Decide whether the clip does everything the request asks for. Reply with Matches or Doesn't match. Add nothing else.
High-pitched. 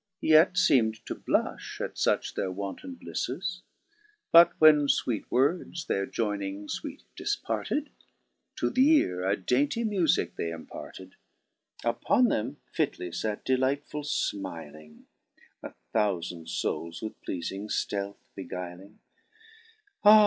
Doesn't match